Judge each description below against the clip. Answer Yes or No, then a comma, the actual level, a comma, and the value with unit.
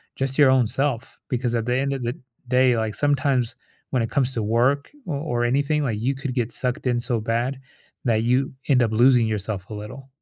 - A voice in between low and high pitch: No, low, 125 Hz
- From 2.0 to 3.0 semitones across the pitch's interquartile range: Yes, average, 2.7 semitones